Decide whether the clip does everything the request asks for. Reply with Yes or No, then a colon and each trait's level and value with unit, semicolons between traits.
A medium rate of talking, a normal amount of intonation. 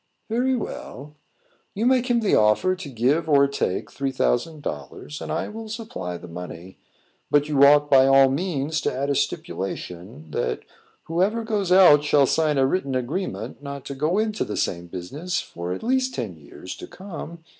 No: average, 180 wpm; wide, 7.7 semitones